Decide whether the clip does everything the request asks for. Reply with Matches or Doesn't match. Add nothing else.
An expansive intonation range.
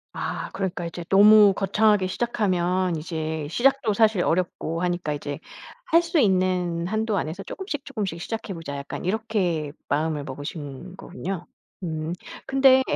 Doesn't match